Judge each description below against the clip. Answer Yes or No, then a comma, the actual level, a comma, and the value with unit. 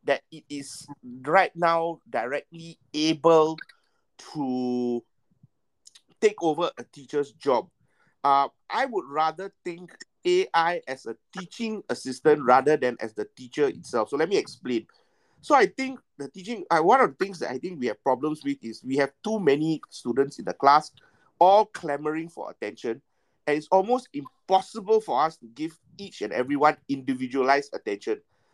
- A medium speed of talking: Yes, average, 160 wpm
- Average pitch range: No, wide, 6.3 semitones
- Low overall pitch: No, medium, 155 Hz